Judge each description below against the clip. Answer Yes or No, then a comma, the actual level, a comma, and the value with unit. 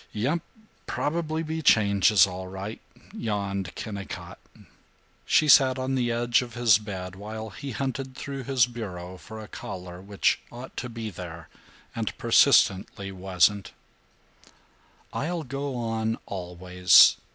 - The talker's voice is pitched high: No, low, 110 Hz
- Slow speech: Yes, slow, 130 wpm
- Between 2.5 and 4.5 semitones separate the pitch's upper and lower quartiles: No, average, 5.3 semitones